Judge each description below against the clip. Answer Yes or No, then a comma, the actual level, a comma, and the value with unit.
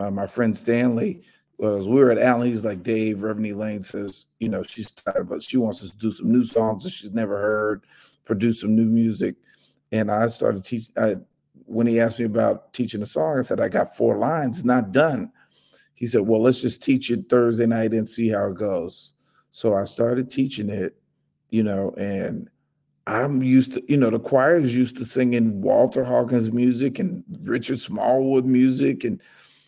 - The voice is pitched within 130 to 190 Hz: No, low, 115 Hz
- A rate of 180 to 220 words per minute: Yes, average, 195 wpm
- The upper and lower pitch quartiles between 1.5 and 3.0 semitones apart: Yes, narrow, 2.6 semitones